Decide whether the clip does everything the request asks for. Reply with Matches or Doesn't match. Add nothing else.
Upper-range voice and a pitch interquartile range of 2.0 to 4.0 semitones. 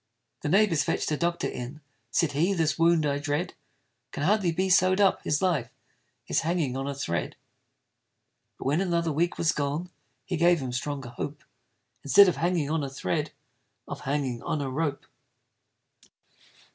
Doesn't match